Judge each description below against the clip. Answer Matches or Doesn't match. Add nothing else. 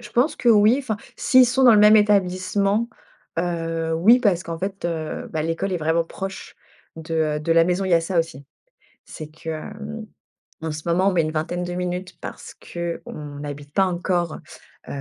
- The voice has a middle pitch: Matches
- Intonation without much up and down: Doesn't match